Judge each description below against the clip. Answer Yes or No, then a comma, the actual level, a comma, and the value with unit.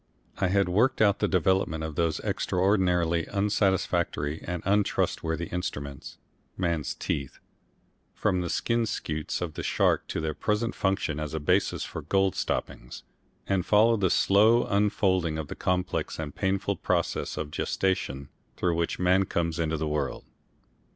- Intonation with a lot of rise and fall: No, average, 3.7 semitones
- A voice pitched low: Yes, very low, 90 Hz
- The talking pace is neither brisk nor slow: Yes, average, 150 wpm